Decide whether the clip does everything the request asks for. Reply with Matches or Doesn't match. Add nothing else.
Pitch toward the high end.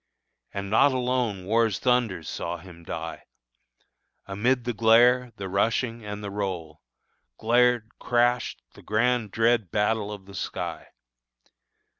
Doesn't match